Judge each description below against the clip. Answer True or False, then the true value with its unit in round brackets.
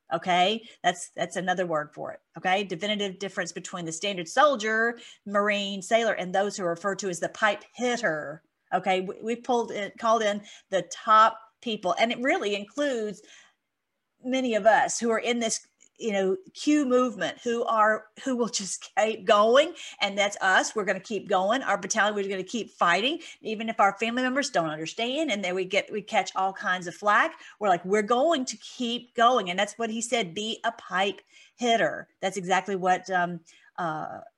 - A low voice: False (210 Hz)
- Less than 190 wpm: False (195 wpm)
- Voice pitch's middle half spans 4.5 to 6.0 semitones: False (3.7 semitones)